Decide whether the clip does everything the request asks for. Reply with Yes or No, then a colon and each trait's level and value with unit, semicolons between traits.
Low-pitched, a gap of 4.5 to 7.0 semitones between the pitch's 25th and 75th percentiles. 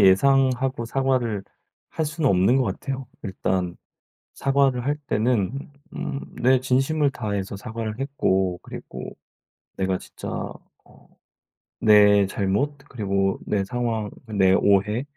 Yes: low, 115 Hz; average, 5.3 semitones